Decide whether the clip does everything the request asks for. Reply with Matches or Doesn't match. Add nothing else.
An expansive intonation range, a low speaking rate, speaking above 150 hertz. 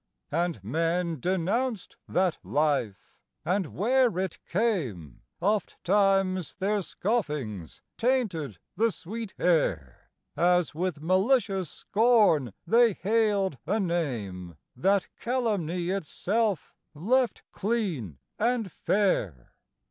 Matches